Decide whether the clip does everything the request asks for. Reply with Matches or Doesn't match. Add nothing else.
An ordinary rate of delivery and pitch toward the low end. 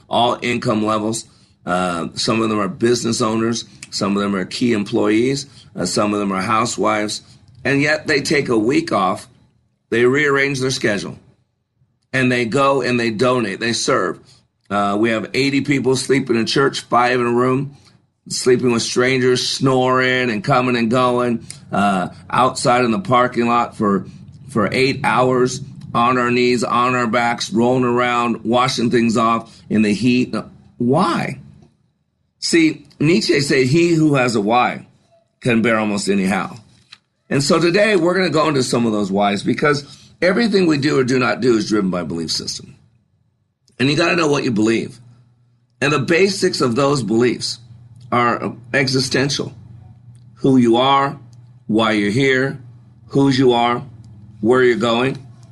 Matches